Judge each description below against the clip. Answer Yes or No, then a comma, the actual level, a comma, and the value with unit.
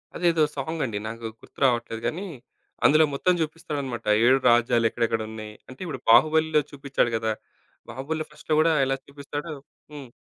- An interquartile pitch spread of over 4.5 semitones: Yes, average, 4.9 semitones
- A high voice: No, medium, 140 Hz